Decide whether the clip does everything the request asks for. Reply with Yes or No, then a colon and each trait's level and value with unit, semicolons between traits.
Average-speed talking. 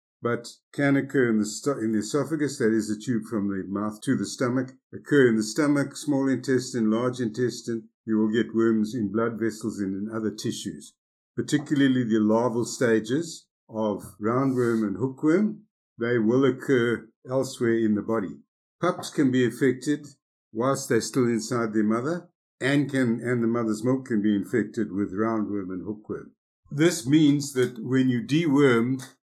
Yes: average, 165 wpm